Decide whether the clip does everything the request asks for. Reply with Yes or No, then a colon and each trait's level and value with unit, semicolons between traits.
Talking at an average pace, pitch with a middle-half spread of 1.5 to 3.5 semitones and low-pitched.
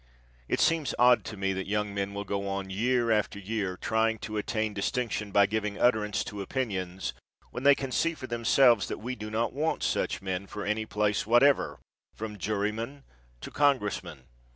Yes: average, 180 wpm; average, 3.2 semitones; low, 105 Hz